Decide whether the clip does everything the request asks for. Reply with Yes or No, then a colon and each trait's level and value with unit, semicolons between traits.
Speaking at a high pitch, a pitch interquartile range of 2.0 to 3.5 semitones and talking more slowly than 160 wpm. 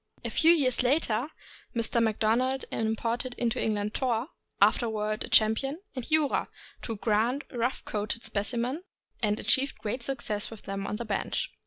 Yes: high, 230 Hz; average, 3.1 semitones; average, 150 wpm